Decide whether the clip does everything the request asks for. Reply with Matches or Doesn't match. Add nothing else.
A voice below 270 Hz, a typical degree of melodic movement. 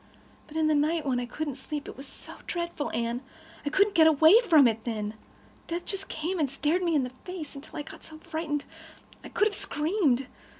Doesn't match